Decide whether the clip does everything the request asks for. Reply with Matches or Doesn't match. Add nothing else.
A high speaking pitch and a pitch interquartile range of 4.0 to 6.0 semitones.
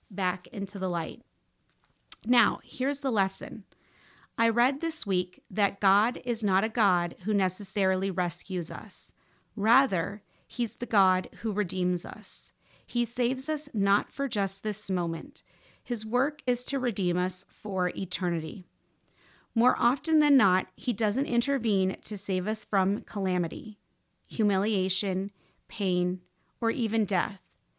Matches